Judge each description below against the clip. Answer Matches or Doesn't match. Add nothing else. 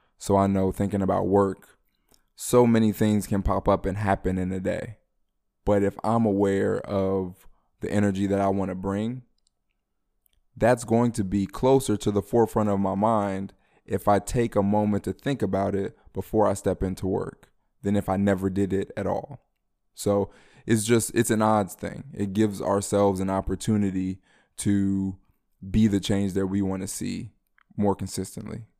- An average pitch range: Doesn't match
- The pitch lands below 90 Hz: Doesn't match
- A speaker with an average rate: Matches